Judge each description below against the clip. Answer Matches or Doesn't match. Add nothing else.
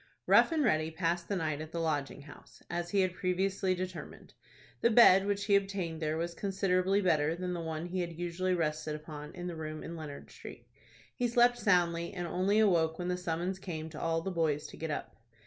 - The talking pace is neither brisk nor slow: Doesn't match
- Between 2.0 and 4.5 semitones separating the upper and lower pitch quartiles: Matches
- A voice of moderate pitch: Matches